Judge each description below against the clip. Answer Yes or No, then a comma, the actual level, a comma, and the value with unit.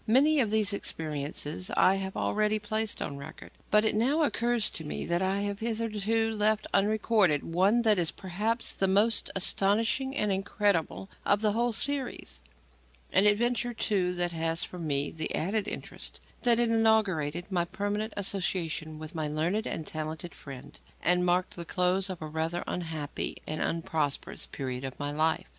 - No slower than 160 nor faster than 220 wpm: Yes, average, 165 wpm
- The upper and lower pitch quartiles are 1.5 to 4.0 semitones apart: No, average, 5.1 semitones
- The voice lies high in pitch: Yes, high, 195 Hz